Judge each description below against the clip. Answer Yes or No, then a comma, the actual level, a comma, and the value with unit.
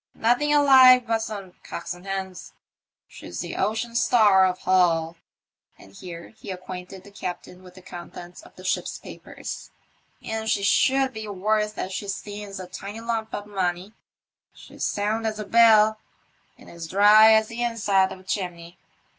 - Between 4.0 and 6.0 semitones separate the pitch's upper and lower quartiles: No, average, 3.2 semitones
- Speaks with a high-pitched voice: Yes, high, 205 Hz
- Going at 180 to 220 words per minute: No, average, 170 wpm